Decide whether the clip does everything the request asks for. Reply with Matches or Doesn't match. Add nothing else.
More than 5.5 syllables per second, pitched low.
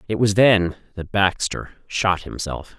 Doesn't match